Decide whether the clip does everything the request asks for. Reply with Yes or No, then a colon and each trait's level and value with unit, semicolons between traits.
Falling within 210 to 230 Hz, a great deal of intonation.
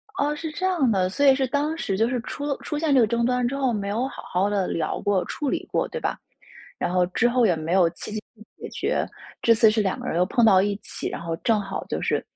Yes: high, 225 Hz; wide, 5.9 semitones